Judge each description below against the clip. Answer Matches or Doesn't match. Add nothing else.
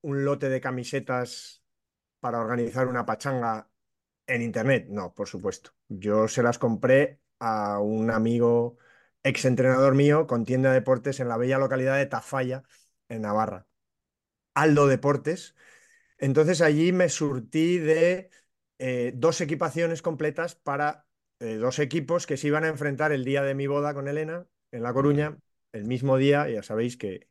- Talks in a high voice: Doesn't match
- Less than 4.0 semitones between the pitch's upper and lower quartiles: Doesn't match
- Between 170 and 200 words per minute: Doesn't match